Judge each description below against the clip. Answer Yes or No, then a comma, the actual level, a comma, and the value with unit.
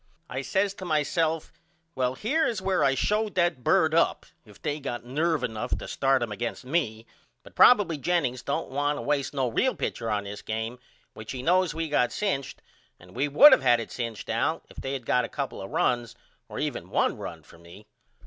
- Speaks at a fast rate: Yes, fast, 215 wpm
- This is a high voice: No, low, 135 Hz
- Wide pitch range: Yes, wide, 5.8 semitones